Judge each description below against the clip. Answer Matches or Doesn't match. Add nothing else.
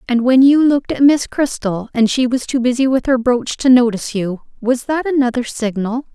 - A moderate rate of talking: Doesn't match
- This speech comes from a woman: Matches